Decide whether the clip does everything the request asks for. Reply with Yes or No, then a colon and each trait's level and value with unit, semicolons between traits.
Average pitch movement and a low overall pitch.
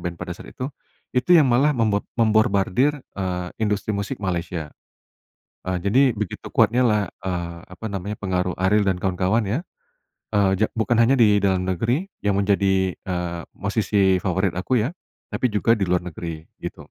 Yes: average, 3.2 semitones; low, 100 Hz